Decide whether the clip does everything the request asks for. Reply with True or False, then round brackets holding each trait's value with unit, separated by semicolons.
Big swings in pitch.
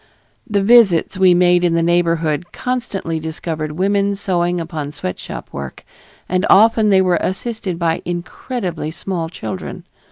False (3.1 semitones)